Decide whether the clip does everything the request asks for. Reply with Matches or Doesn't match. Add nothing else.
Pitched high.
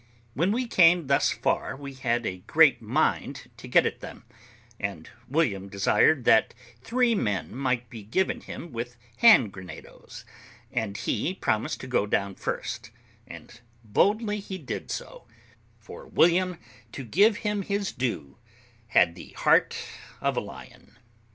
Doesn't match